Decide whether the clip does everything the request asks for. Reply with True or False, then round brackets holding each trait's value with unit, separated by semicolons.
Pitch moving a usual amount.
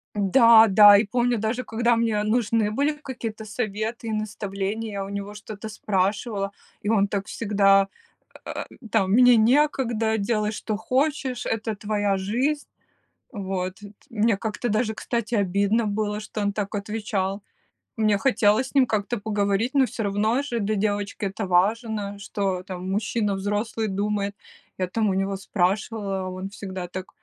False (2.3 semitones)